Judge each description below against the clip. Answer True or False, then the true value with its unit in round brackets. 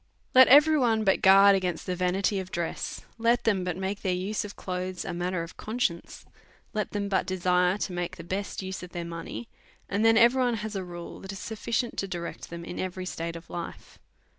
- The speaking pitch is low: False (190 Hz)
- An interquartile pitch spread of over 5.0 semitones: False (3.0 semitones)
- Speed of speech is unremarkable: False (230 wpm)